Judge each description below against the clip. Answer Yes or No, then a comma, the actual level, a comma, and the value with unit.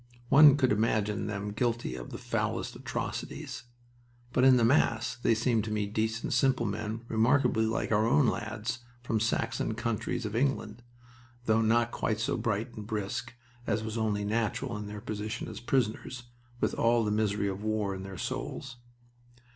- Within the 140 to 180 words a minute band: Yes, average, 170 wpm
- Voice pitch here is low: Yes, low, 110 Hz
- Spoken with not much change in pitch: Yes, narrow, 2.0 semitones